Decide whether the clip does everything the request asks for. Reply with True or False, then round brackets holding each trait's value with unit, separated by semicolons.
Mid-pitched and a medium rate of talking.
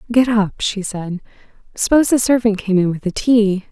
False (215 Hz; 195 wpm)